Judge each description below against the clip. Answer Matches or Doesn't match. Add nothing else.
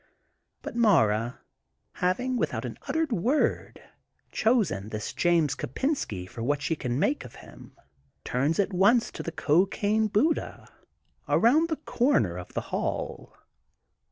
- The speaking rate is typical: Doesn't match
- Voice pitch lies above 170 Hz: Matches